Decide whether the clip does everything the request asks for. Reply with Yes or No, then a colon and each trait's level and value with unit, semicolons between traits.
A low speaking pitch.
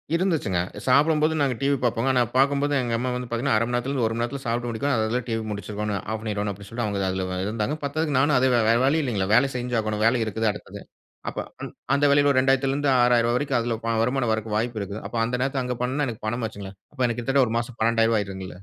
Yes: low, 120 Hz